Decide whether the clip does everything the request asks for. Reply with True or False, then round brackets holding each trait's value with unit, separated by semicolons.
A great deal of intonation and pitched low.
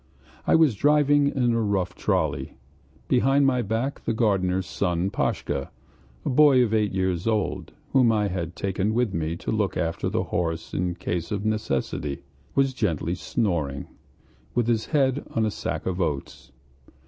True (5.7 semitones; 105 Hz)